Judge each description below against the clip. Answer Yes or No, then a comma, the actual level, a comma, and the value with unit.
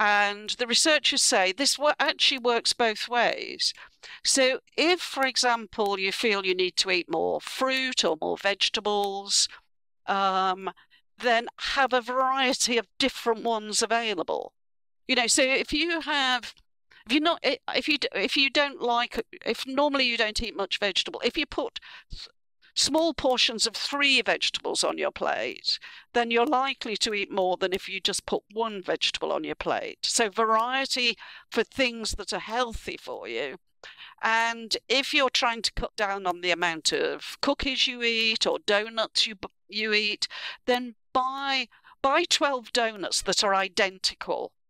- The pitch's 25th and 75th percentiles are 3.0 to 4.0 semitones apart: No, average, 4.4 semitones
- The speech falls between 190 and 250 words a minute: No, average, 160 wpm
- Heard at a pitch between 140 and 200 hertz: No, high, 240 Hz